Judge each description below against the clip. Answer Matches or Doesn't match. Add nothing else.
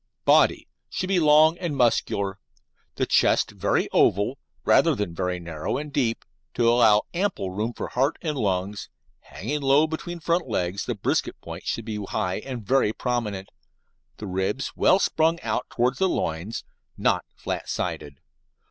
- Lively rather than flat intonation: Matches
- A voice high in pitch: Doesn't match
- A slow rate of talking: Doesn't match